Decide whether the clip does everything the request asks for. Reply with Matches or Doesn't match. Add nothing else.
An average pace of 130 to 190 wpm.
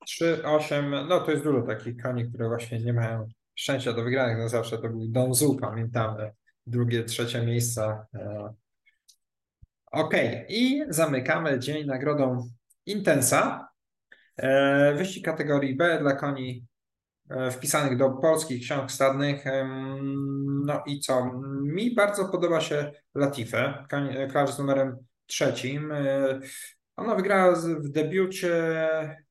Doesn't match